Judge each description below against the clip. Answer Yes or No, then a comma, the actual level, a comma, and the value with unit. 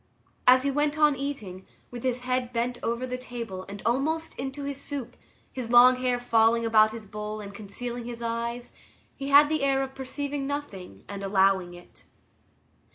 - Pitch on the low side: No, high, 245 Hz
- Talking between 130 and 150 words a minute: No, average, 175 wpm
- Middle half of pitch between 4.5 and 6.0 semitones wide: No, average, 3.9 semitones